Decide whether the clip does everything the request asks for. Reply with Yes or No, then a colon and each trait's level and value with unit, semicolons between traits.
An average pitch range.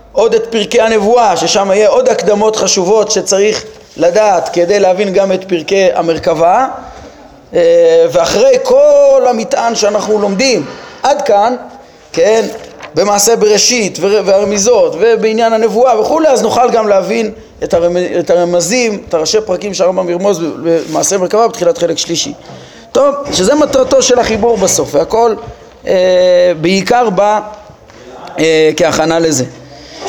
Yes: average, 4.7 semitones